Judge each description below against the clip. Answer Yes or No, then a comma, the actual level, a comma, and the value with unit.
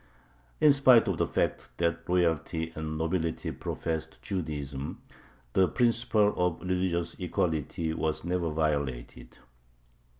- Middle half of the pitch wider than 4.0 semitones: No, average, 2.7 semitones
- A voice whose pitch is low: Yes, very low, 85 Hz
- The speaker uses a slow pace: Yes, slow, 110 wpm